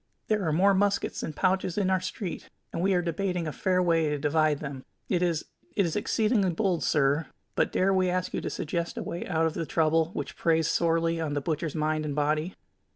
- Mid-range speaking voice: Yes, medium, 165 Hz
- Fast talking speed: Yes, fast, 220 wpm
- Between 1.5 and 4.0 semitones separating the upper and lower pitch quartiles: Yes, average, 3.0 semitones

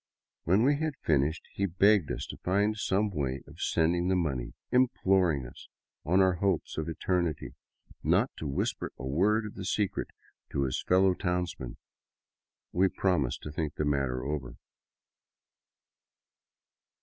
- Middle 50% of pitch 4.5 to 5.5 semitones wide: Yes, average, 4.9 semitones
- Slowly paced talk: No, average, 145 wpm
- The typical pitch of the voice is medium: No, very low, 90 Hz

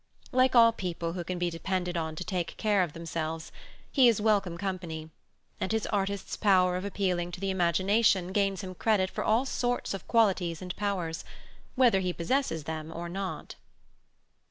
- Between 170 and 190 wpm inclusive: Yes, average, 175 wpm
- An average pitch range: Yes, average, 3.2 semitones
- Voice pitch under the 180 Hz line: No, medium, 185 Hz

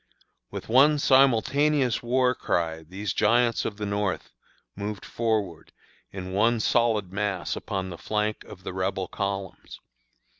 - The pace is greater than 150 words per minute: No, slow, 135 wpm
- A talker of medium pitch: No, low, 105 Hz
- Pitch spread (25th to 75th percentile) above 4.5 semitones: No, average, 3.8 semitones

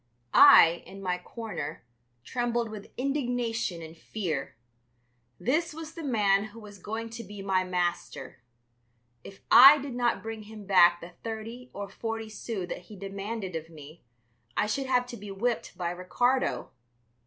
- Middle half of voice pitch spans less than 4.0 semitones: No, average, 4.7 semitones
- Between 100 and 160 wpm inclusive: Yes, average, 155 wpm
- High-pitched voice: Yes, high, 215 Hz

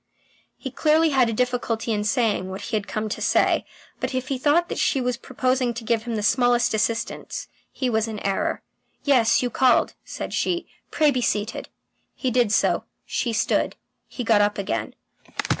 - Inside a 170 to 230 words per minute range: Yes, average, 185 wpm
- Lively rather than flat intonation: No, average, 2.8 semitones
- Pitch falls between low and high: No, high, 240 Hz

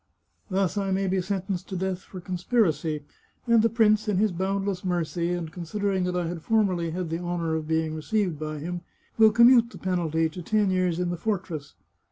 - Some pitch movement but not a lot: Yes, average, 3.1 semitones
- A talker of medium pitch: Yes, medium, 180 Hz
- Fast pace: Yes, fast, 210 wpm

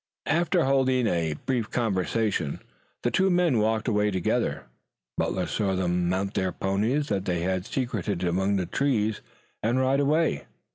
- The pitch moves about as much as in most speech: No, wide, 5.9 semitones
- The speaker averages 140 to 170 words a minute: Yes, average, 155 wpm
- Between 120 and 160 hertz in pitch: No, low, 105 Hz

